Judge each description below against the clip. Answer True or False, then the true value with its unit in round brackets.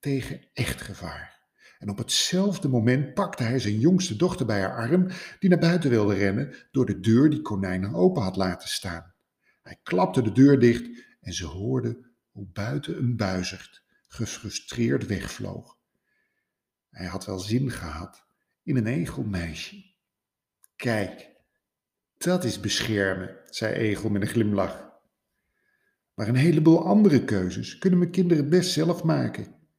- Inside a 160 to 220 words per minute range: False (145 wpm)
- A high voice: False (120 Hz)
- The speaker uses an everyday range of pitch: False (8.5 semitones)